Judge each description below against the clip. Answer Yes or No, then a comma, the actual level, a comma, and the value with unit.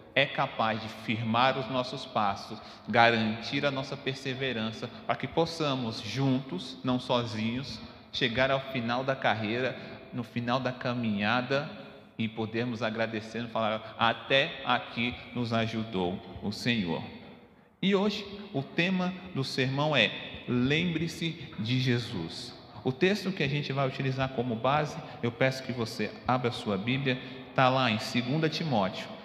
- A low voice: Yes, low, 125 Hz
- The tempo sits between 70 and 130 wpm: No, average, 140 wpm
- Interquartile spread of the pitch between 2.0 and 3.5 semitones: Yes, average, 3.0 semitones